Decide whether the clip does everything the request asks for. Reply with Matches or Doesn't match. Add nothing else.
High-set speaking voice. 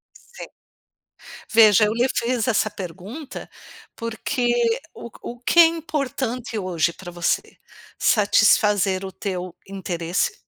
Matches